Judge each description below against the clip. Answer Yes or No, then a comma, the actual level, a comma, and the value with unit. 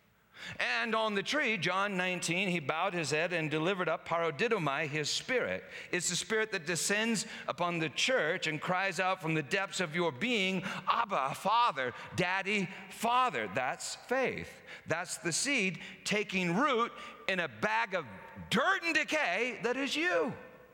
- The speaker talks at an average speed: Yes, average, 155 wpm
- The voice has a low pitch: No, high, 190 Hz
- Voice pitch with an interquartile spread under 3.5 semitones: No, average, 4.3 semitones